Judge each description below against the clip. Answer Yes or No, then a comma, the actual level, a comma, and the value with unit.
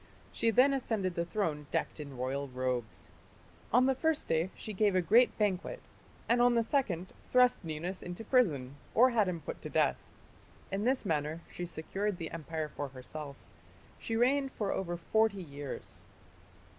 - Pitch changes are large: Yes, wide, 7.1 semitones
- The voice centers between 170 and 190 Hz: Yes, medium, 185 Hz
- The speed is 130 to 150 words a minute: No, average, 170 wpm